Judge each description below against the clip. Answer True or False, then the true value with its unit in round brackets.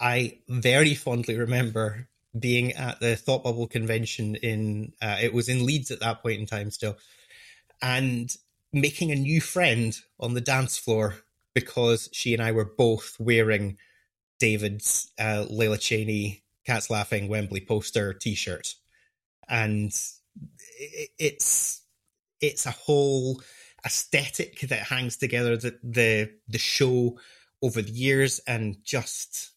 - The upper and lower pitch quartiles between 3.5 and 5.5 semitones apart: False (2.8 semitones)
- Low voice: True (115 Hz)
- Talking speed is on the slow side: True (130 wpm)